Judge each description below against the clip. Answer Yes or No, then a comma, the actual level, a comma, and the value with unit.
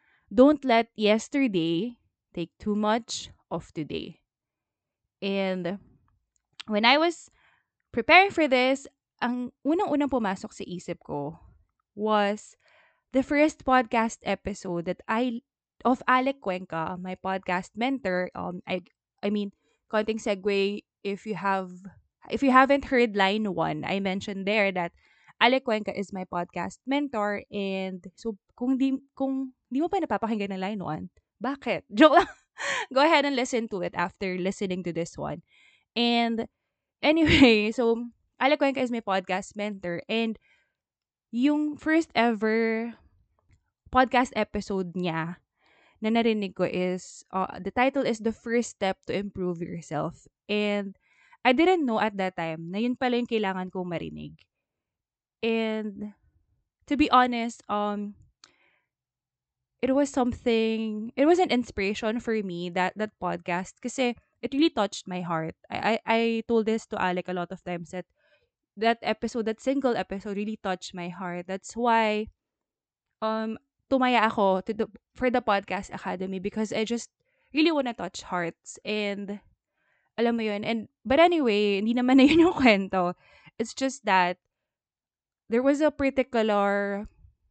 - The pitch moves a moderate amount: Yes, average, 4.8 semitones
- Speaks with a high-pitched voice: Yes, high, 215 Hz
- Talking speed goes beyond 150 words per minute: No, average, 145 wpm